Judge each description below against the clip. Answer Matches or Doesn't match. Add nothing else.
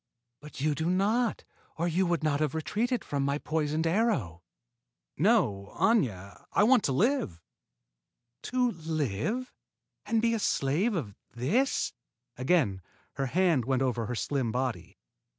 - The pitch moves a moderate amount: Doesn't match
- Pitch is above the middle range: Doesn't match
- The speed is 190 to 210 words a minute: Doesn't match